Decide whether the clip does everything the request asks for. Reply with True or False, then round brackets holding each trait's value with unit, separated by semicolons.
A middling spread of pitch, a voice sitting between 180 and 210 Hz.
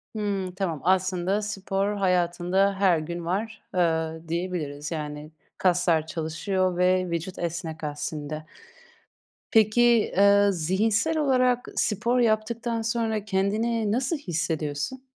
True (4.5 semitones; 185 Hz)